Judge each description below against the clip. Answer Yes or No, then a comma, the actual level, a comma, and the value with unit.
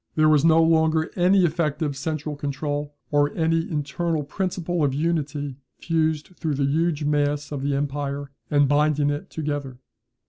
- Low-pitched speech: No, medium, 150 Hz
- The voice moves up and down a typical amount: No, narrow, 2.0 semitones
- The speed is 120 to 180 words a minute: Yes, average, 150 wpm